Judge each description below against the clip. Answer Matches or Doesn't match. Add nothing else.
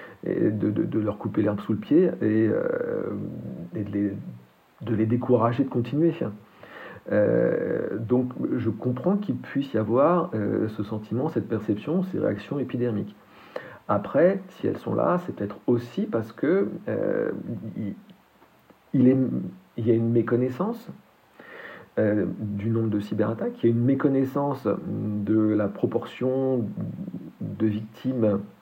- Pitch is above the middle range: Doesn't match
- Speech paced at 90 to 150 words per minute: Matches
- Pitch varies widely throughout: Doesn't match